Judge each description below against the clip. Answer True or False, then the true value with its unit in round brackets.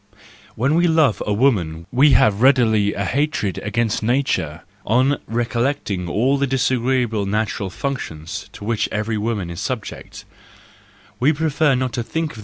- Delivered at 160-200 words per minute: False (150 wpm)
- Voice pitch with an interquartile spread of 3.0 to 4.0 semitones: False (4.8 semitones)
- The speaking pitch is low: True (120 Hz)